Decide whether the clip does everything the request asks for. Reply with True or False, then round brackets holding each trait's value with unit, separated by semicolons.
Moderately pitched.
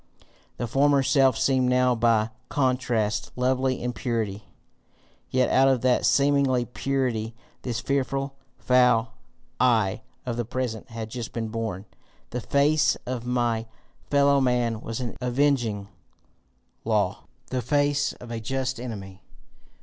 False (125 Hz)